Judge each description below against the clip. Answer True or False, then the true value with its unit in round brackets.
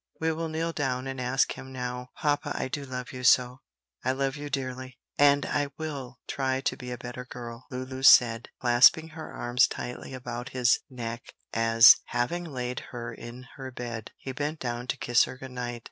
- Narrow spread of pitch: True (1.9 semitones)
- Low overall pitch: True (125 Hz)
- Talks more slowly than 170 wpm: False (190 wpm)